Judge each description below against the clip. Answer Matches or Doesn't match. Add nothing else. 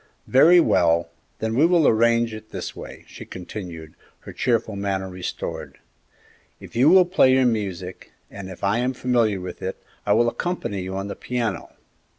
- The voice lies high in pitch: Doesn't match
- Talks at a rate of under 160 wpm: Doesn't match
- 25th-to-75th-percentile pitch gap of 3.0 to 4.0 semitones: Doesn't match